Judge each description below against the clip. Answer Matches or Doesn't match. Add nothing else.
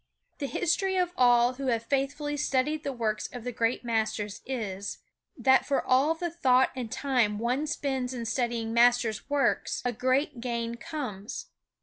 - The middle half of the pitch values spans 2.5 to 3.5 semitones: Matches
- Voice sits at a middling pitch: Doesn't match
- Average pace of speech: Matches